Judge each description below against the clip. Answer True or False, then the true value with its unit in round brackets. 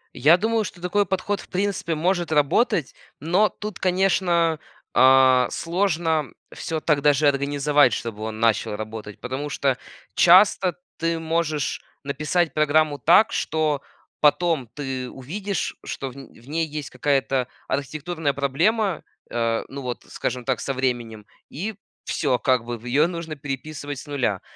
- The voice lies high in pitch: False (150 Hz)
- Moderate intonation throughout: True (4.5 semitones)